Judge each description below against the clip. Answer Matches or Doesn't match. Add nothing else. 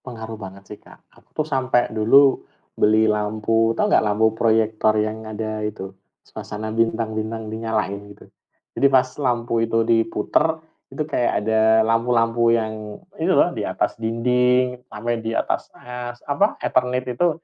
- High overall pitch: Doesn't match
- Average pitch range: Doesn't match